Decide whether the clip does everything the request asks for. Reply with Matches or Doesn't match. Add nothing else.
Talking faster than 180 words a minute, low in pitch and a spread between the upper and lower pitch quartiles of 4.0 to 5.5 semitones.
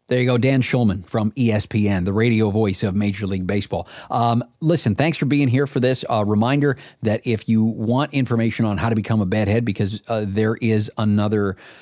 Doesn't match